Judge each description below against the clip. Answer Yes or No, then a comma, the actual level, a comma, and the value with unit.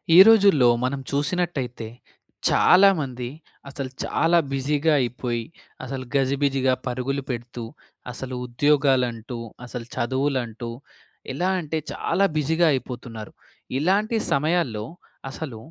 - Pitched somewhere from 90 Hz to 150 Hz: Yes, low, 135 Hz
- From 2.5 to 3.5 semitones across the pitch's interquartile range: No, average, 3.9 semitones